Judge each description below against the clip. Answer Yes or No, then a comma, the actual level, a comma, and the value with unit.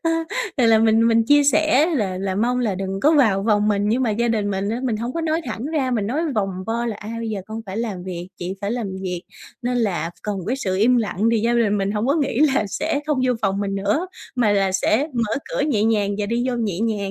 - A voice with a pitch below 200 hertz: No, high, 220 Hz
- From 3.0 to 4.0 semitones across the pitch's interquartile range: Yes, average, 3.6 semitones